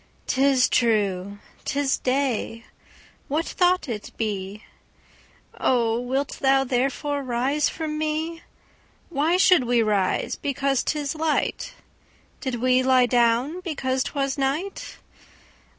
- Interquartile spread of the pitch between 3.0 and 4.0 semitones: Yes, average, 3.7 semitones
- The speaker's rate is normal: No, slow, 100 wpm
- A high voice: Yes, very high, 265 Hz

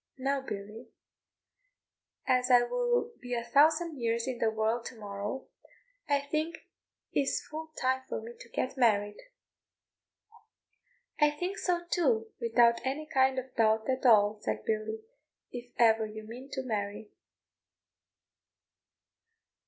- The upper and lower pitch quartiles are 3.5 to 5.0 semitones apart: Yes, average, 4.0 semitones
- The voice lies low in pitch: No, high, 245 Hz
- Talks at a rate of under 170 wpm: Yes, slow, 135 wpm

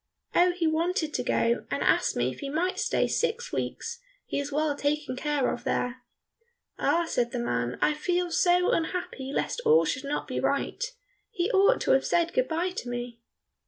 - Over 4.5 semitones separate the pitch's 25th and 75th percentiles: Yes, average, 5.2 semitones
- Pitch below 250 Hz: No, very high, 315 Hz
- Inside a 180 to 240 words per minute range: Yes, average, 195 wpm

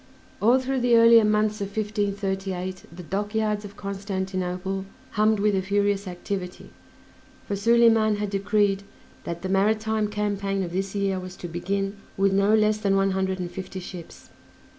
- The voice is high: Yes, high, 200 Hz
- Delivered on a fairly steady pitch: Yes, narrow, 1.8 semitones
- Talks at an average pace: Yes, average, 160 wpm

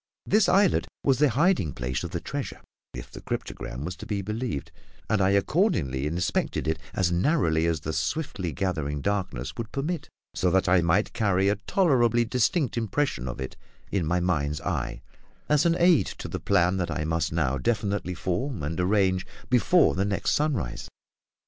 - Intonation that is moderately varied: No, wide, 7.4 semitones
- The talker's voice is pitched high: No, very low, 95 Hz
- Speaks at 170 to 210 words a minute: Yes, average, 175 wpm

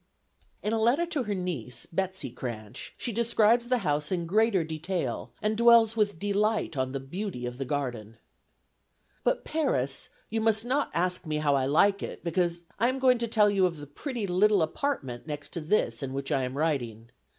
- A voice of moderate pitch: Yes, medium, 180 Hz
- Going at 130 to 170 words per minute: No, average, 195 wpm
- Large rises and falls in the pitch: Yes, wide, 8.0 semitones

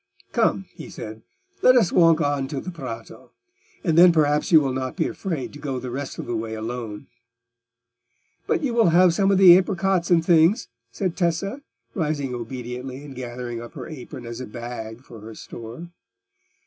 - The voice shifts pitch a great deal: Yes, wide, 6.0 semitones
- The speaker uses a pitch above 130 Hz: Yes, medium, 140 Hz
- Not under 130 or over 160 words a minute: No, average, 185 wpm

